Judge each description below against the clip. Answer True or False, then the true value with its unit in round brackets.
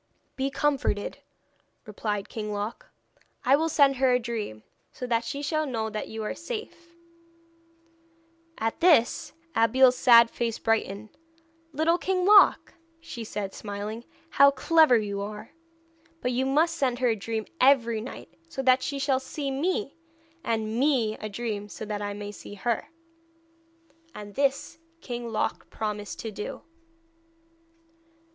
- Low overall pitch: False (235 Hz)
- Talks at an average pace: True (145 wpm)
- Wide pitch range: False (4.5 semitones)